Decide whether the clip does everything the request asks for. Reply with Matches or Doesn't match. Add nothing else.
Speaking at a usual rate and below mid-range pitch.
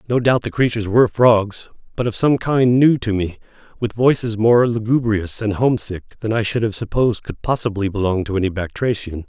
Matches